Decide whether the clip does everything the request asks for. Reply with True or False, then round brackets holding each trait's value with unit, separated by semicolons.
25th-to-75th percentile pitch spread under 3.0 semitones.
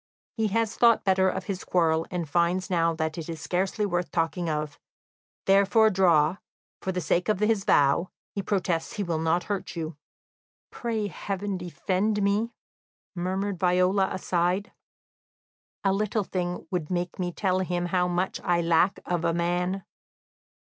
True (2.4 semitones)